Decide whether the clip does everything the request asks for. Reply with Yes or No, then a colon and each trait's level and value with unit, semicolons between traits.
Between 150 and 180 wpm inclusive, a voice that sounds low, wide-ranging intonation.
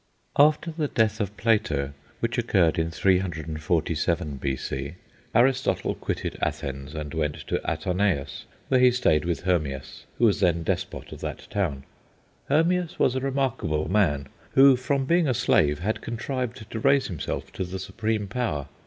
Yes: average, 155 wpm; very low, 95 Hz; wide, 8.4 semitones